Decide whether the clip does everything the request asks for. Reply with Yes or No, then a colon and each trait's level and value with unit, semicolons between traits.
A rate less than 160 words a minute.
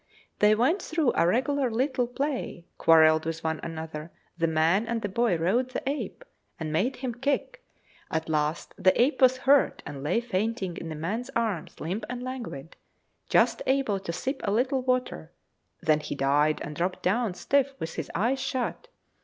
No: average, 180 wpm